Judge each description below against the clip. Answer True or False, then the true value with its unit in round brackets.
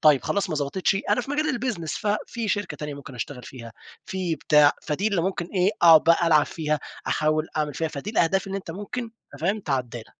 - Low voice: False (165 Hz)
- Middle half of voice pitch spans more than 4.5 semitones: True (4.9 semitones)